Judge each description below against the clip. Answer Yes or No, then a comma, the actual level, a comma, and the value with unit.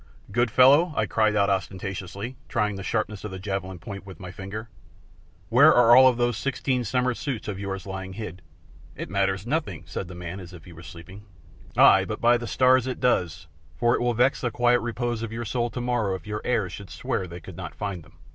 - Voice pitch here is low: Yes, low, 105 Hz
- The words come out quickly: Yes, fast, 220 wpm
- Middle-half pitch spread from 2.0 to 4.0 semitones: No, average, 4.4 semitones